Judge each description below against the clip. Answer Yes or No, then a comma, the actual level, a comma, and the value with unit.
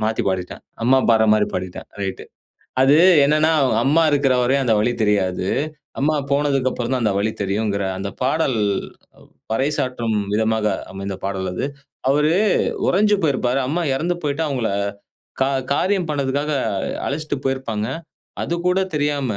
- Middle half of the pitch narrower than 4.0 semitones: No, wide, 5.4 semitones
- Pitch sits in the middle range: No, low, 130 Hz